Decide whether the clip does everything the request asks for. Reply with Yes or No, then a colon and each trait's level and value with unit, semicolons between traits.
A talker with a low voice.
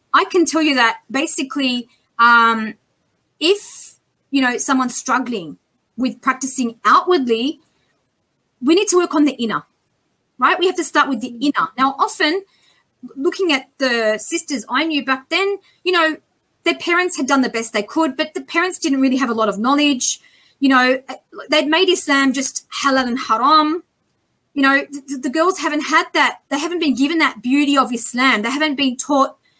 No: very high, 280 Hz